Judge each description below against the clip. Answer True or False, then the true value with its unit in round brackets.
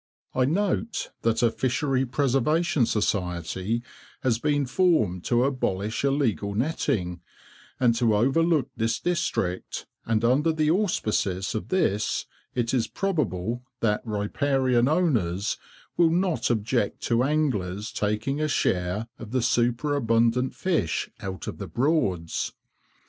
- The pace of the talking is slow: True (120 wpm)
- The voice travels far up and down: True (5.7 semitones)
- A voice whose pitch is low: True (120 Hz)